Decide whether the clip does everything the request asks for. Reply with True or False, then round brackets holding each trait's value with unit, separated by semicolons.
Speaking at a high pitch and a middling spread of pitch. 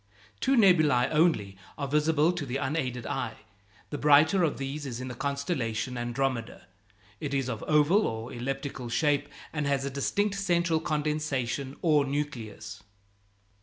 False (140 Hz; 3.4 semitones)